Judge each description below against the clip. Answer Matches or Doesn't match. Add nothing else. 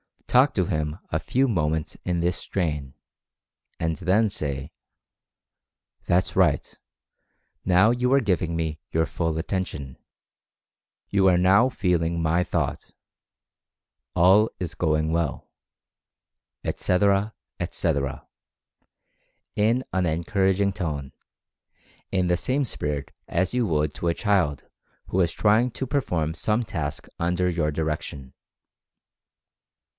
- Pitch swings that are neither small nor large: Matches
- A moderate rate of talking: Doesn't match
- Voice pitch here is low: Matches